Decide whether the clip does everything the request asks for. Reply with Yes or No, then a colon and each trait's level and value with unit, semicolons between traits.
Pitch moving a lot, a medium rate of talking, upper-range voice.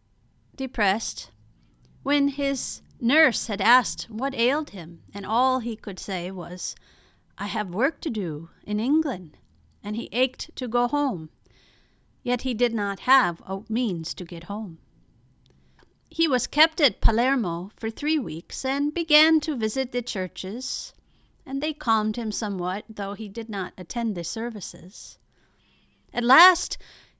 Yes: wide, 6.3 semitones; average, 145 wpm; high, 225 Hz